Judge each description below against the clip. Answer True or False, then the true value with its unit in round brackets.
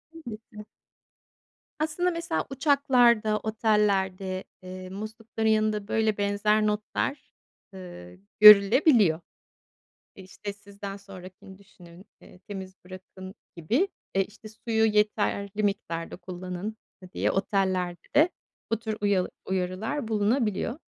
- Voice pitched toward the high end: True (205 Hz)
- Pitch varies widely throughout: False (2.8 semitones)